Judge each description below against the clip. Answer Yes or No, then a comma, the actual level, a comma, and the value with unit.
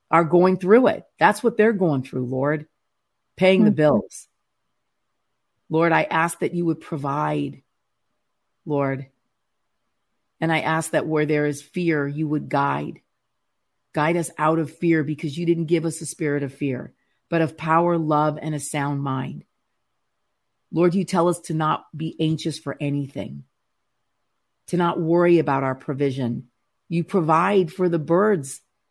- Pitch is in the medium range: Yes, medium, 160 Hz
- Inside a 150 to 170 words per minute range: Yes, average, 155 wpm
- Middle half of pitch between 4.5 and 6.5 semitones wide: No, average, 2.9 semitones